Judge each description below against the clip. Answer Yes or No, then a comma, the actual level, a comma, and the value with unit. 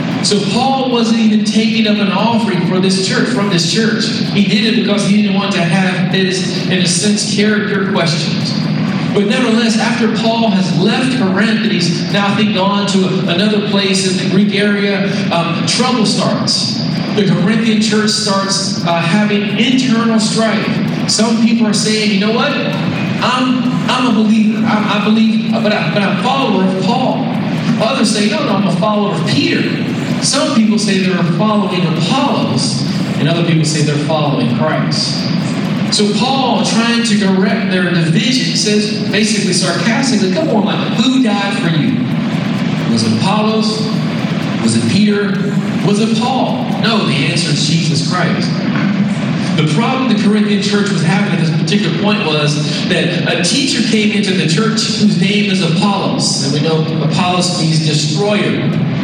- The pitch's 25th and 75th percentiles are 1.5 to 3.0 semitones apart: Yes, narrow, 2.6 semitones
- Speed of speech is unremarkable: Yes, average, 170 wpm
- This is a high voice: Yes, high, 205 Hz